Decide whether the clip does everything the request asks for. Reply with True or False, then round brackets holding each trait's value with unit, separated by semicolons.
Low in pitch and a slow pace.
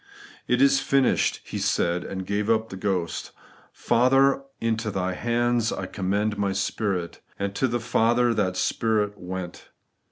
False (105 Hz; 155 wpm)